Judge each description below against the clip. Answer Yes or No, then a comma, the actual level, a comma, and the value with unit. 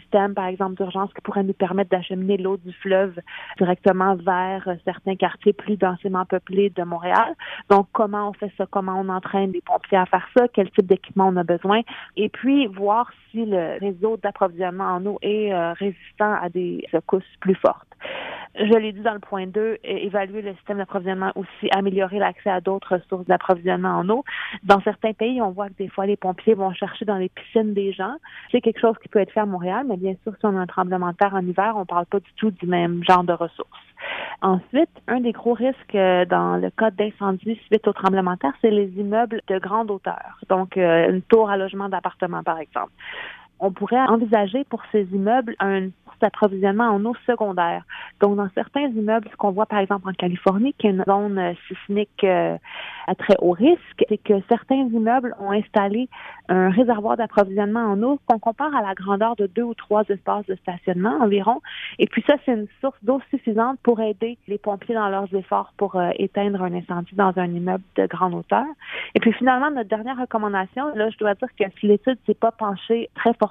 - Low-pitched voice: No, high, 200 Hz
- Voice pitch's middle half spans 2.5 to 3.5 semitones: Yes, average, 2.9 semitones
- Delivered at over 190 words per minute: Yes, average, 205 wpm